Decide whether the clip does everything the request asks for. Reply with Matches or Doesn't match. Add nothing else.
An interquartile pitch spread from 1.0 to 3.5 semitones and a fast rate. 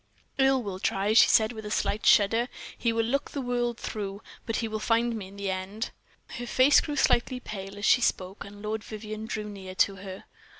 Matches